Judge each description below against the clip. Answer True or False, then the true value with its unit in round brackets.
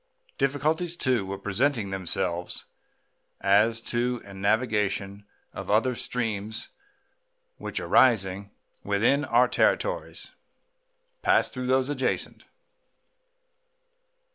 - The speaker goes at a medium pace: False (90 wpm)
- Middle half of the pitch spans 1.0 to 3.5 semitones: False (4.5 semitones)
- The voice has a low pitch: True (110 Hz)